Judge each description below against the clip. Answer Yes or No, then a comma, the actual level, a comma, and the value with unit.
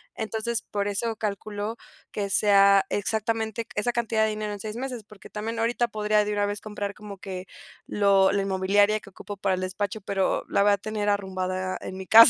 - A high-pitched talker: Yes, high, 205 Hz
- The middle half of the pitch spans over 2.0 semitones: No, narrow, 1.7 semitones